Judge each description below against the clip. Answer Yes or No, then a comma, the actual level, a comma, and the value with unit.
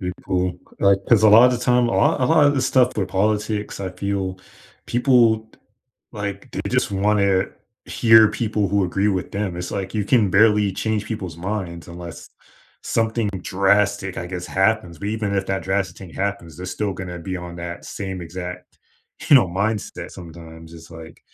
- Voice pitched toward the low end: Yes, low, 100 Hz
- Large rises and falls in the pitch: No, average, 3.1 semitones